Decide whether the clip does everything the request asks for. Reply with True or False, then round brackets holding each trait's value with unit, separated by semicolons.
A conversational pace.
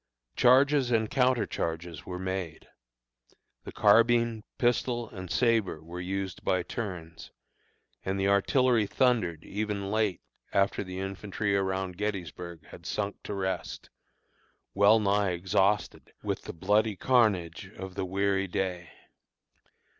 False (125 wpm)